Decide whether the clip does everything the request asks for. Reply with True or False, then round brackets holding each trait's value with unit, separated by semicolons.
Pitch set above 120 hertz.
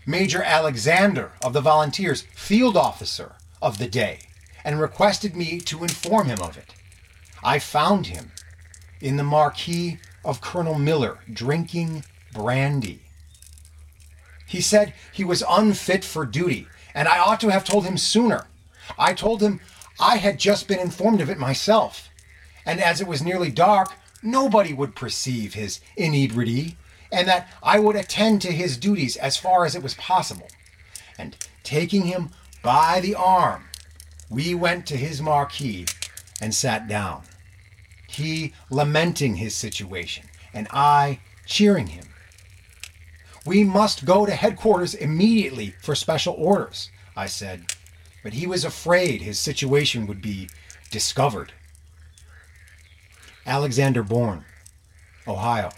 True (135 Hz)